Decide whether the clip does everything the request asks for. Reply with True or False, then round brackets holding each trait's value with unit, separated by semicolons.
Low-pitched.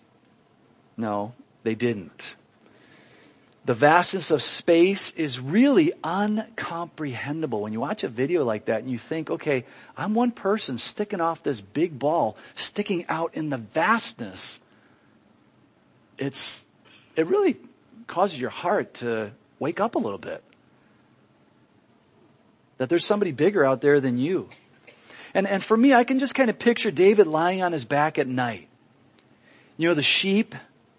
False (165 Hz)